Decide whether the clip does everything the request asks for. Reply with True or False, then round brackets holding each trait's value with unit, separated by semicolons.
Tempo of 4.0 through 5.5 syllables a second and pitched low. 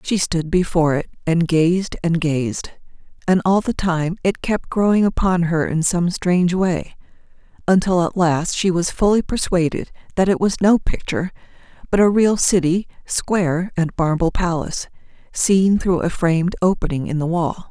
False (4.7 syllables/s; 175 Hz)